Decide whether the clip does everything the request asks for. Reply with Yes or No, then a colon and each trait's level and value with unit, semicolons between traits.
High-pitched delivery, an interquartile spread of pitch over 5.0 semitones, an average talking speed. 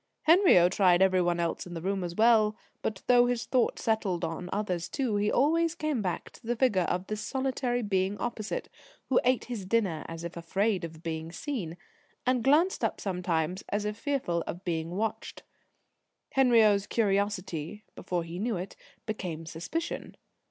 Yes: high, 205 Hz; wide, 5.5 semitones; average, 170 wpm